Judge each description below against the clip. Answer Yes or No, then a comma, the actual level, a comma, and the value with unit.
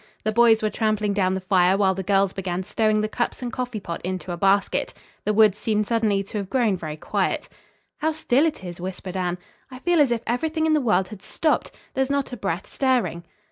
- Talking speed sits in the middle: No, fast, 225 wpm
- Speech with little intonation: No, average, 4.5 semitones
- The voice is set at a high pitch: Yes, high, 210 Hz